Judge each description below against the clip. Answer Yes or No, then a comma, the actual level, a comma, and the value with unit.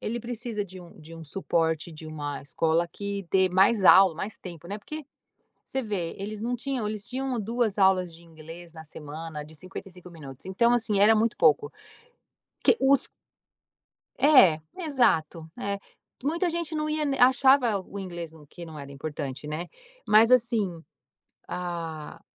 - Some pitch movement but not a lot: No, wide, 6.2 semitones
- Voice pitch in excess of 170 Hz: Yes, high, 190 Hz